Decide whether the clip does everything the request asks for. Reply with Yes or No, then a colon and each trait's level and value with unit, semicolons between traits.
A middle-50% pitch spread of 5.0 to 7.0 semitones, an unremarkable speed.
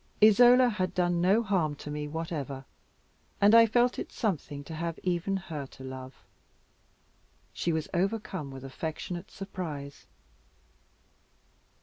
No: average, 5.3 semitones; slow, 125 wpm